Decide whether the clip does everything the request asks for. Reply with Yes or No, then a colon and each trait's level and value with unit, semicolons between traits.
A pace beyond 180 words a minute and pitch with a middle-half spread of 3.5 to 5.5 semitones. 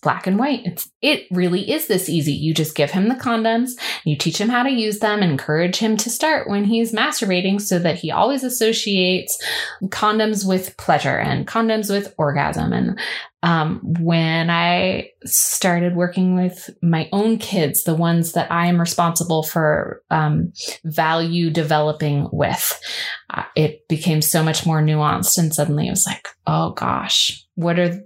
No: average, 170 wpm; average, 4.7 semitones